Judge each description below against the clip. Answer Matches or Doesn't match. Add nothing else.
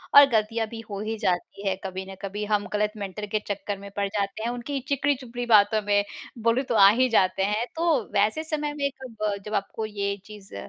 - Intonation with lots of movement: Doesn't match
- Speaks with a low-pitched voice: Doesn't match